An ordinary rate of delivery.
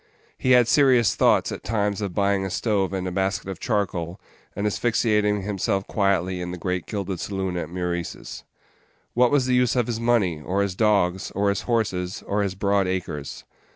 Yes: average, 190 wpm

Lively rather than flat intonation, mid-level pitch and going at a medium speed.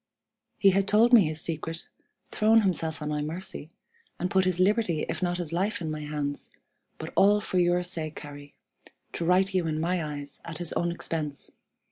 No: average, 3.5 semitones; medium, 170 Hz; average, 190 wpm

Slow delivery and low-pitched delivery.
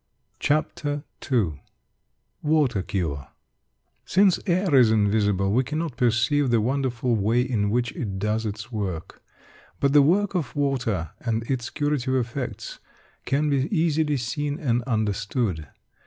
Yes: slow, 130 wpm; low, 125 Hz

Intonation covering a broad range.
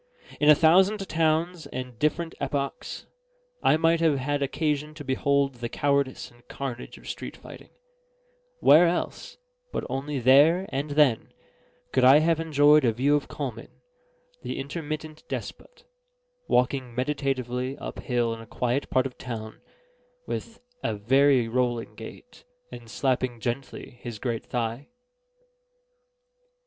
No: average, 3.6 semitones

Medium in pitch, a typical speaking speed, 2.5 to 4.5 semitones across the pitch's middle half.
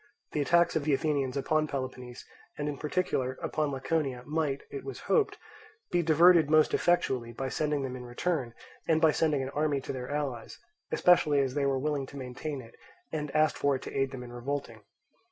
Yes: medium, 145 Hz; average, 195 wpm; average, 2.9 semitones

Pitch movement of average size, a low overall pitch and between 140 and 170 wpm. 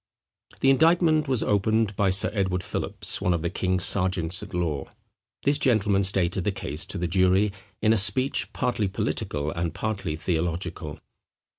Yes: average, 3.9 semitones; very low, 95 Hz; average, 160 wpm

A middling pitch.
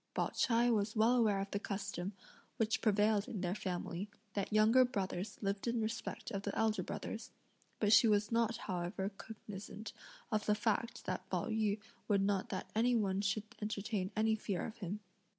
No: high, 210 Hz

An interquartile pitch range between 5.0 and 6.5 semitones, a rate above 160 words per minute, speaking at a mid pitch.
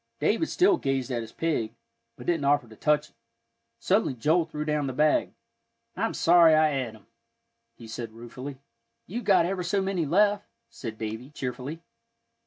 Yes: wide, 5.6 semitones; average, 170 wpm; medium, 150 Hz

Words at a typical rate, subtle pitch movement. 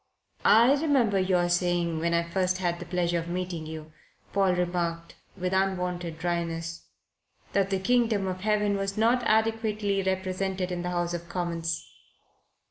Yes: average, 150 wpm; narrow, 2.3 semitones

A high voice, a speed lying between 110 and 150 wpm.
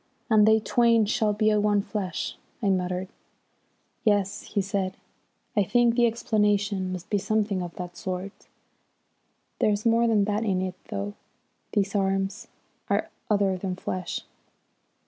Yes: high, 205 Hz; average, 140 wpm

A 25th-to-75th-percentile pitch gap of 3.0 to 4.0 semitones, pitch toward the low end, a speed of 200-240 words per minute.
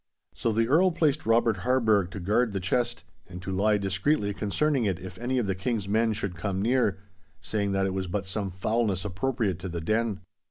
Yes: average, 3.7 semitones; low, 105 Hz; fast, 205 wpm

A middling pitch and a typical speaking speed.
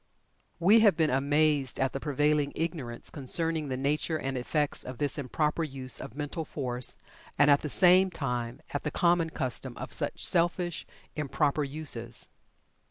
Yes: medium, 145 Hz; average, 160 wpm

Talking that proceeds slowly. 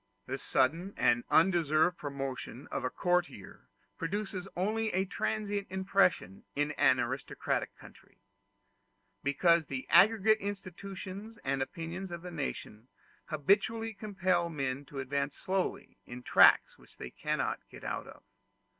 Yes: slow, 130 wpm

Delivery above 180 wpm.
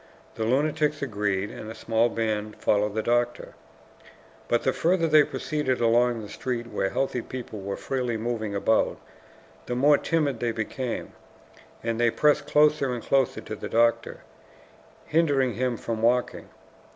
No: average, 150 wpm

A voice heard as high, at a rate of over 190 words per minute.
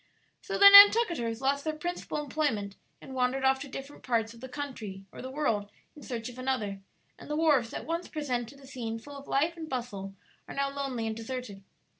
Yes: very high, 265 Hz; fast, 205 wpm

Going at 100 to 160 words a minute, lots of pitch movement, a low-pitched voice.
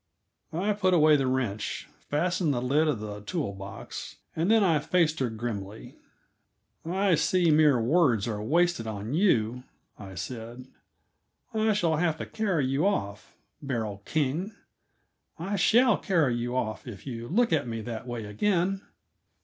No: average, 155 wpm; wide, 7.5 semitones; medium, 145 Hz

